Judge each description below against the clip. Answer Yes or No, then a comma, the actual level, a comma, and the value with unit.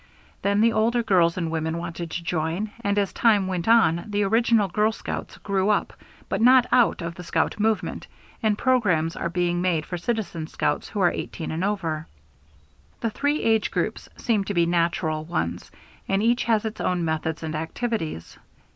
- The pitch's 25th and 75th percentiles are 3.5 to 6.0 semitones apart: Yes, average, 4.8 semitones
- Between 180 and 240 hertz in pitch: Yes, high, 190 Hz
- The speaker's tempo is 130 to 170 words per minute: No, average, 180 wpm